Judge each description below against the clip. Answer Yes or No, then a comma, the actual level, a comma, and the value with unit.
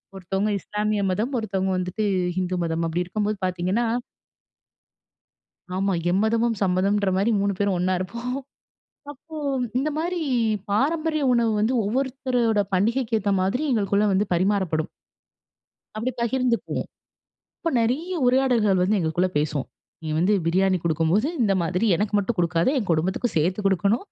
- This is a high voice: Yes, high, 205 Hz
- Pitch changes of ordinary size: Yes, average, 4.3 semitones